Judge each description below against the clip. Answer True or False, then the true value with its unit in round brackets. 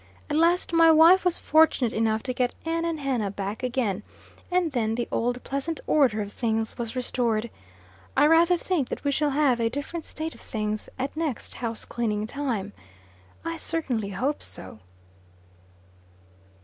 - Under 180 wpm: True (160 wpm)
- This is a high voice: True (255 Hz)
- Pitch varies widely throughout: True (6.2 semitones)